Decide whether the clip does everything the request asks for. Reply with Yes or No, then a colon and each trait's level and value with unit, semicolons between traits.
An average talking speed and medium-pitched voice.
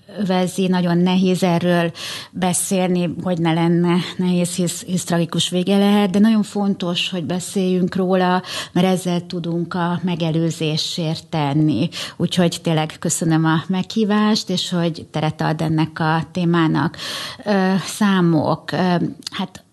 Yes: average, 120 wpm; medium, 175 Hz